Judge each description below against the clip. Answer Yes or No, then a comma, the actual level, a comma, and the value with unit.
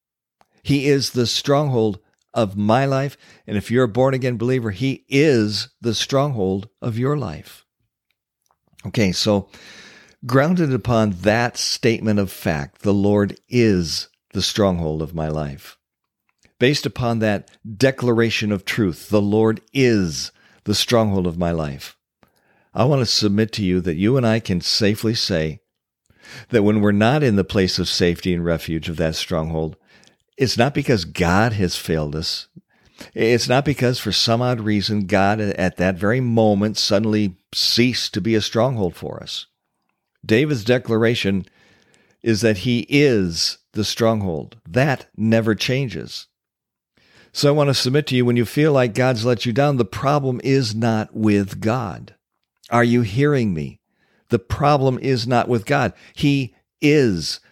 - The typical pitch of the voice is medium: No, low, 110 Hz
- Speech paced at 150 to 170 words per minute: Yes, average, 155 wpm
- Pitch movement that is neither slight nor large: Yes, average, 4.1 semitones